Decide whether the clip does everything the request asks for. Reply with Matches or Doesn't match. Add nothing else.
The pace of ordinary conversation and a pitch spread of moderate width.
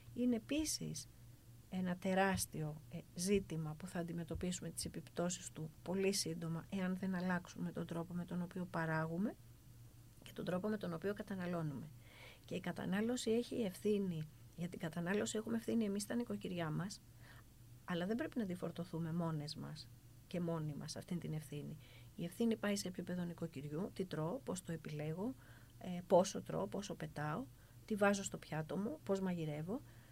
Matches